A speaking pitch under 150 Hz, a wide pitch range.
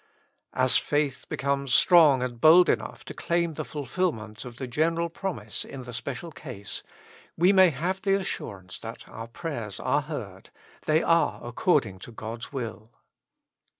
Yes: medium, 140 Hz; wide, 6.4 semitones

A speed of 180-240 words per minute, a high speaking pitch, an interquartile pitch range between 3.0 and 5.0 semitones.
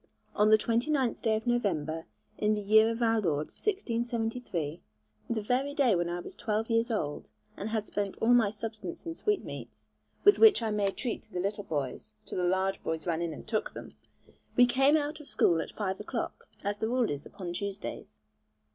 Yes: average, 200 wpm; high, 215 Hz; average, 4.4 semitones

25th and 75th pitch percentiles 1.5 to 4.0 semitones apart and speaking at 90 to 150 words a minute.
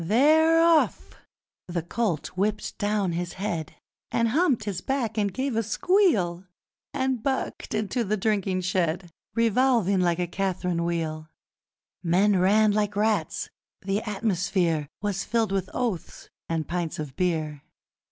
No: average, 4.4 semitones; slow, 135 wpm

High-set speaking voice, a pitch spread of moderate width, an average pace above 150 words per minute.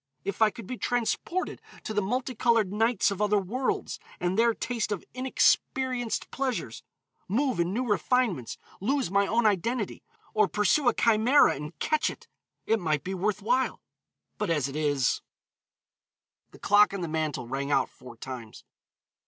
No: high, 210 Hz; wide, 5.8 semitones; average, 160 wpm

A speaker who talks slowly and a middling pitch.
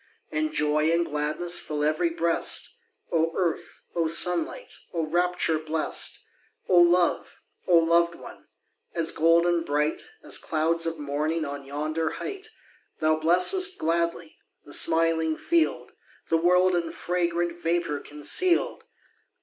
Yes: slow, 125 wpm; medium, 165 Hz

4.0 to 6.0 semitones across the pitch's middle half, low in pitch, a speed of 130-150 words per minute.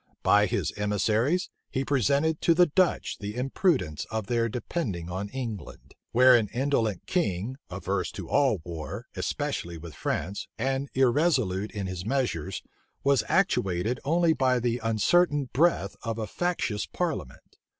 Yes: wide, 5.6 semitones; low, 120 Hz; average, 140 wpm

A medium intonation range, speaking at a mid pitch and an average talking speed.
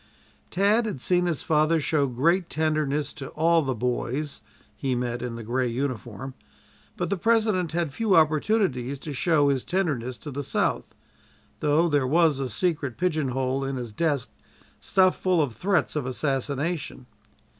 Yes: average, 4.6 semitones; medium, 145 Hz; average, 155 wpm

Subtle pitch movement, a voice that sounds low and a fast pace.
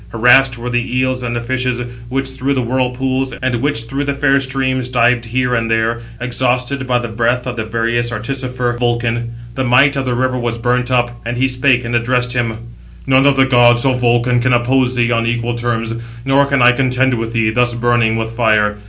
Yes: narrow, 1.6 semitones; low, 125 Hz; fast, 210 wpm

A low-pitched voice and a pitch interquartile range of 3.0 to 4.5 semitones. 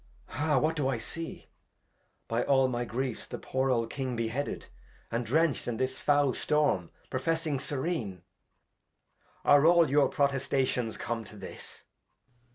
Yes: low, 130 Hz; average, 3.5 semitones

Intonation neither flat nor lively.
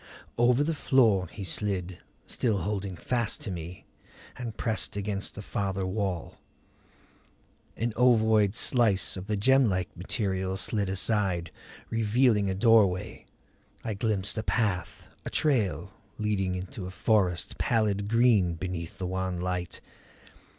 Yes: average, 3.2 semitones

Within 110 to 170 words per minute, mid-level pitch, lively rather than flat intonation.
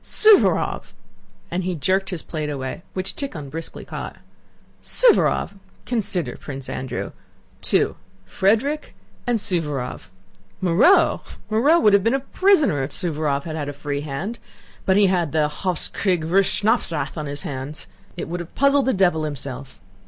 Yes: average, 155 wpm; medium, 175 Hz; wide, 6.3 semitones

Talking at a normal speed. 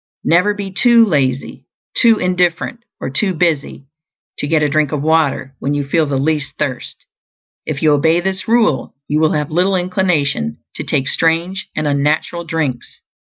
Yes: average, 165 wpm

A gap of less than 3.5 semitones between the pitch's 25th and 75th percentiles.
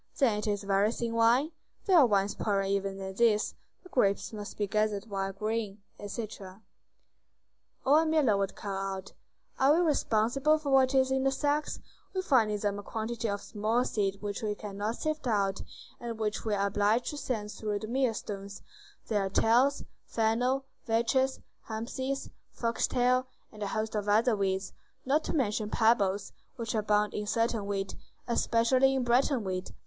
No: average, 3.9 semitones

